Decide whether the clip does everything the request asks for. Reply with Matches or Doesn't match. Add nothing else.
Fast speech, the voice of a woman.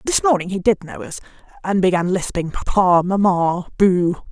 Doesn't match